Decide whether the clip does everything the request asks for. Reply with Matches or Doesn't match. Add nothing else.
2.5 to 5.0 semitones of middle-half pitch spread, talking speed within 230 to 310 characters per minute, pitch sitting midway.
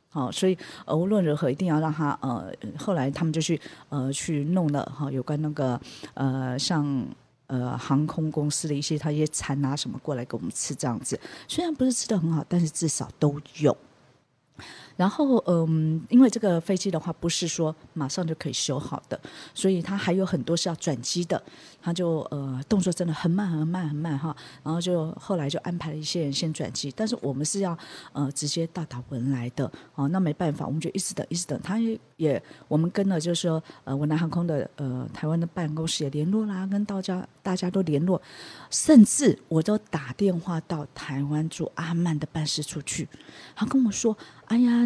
Matches